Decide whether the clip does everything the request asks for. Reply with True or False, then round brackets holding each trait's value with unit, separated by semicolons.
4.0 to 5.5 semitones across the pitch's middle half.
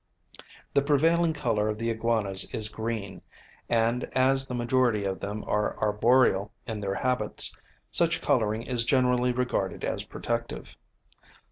False (3.3 semitones)